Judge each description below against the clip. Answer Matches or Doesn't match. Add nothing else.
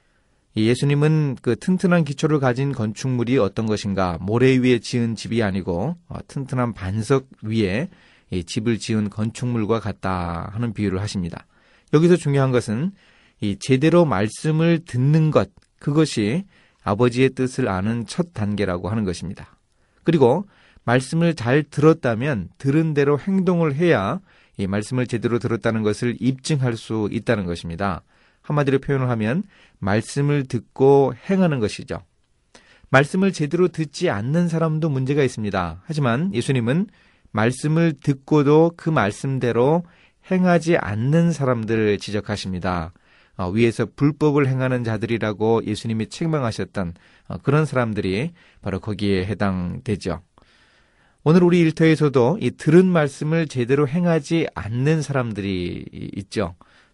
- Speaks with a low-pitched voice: Matches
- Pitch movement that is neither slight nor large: Doesn't match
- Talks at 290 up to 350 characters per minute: Matches